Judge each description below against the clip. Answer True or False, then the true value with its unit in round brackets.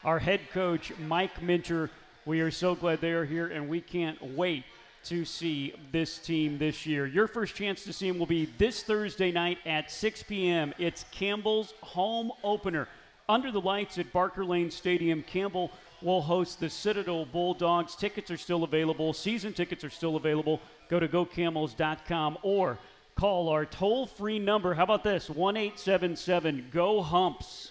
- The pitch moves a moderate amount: True (3.2 semitones)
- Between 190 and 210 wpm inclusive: False (170 wpm)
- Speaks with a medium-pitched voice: True (175 Hz)